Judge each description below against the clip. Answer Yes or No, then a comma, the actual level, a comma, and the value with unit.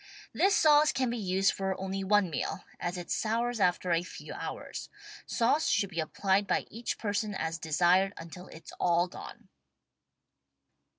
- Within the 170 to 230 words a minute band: No, average, 160 wpm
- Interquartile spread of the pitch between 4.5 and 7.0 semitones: No, average, 3.9 semitones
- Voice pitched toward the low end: No, high, 195 Hz